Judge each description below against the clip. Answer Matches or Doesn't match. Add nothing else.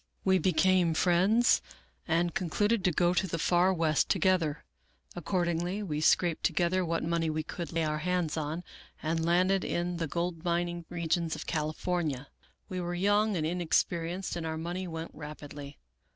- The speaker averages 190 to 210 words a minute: Doesn't match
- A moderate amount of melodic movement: Doesn't match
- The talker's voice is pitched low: Doesn't match